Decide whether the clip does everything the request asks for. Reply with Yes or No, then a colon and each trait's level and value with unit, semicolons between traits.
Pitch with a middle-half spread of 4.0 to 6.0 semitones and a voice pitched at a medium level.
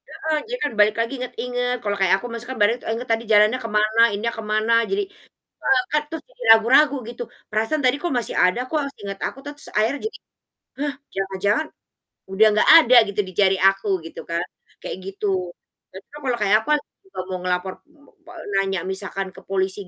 No: average, 4.4 semitones; high, 215 Hz